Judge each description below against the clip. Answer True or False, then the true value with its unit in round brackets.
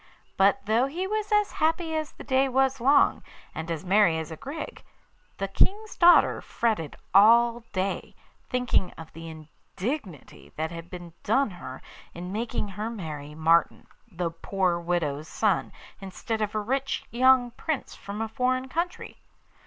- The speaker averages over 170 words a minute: False (155 wpm)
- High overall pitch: True (215 Hz)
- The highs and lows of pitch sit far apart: True (7.4 semitones)